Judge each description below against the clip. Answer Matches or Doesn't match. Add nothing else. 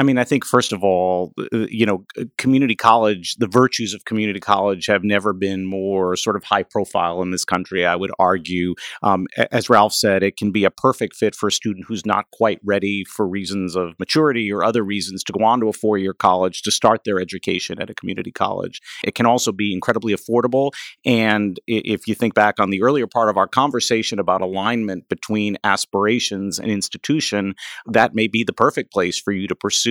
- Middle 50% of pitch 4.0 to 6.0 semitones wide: Doesn't match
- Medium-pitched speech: Doesn't match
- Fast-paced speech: Matches